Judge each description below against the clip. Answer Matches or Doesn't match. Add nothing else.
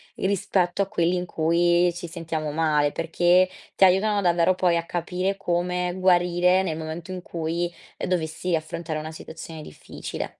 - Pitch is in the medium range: Matches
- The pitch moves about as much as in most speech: Doesn't match